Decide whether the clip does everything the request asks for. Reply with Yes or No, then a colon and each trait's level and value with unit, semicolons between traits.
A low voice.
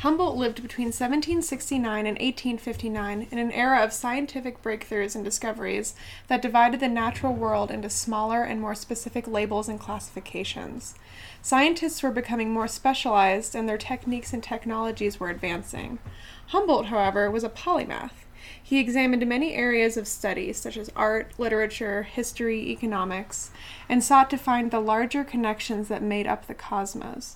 No: high, 230 Hz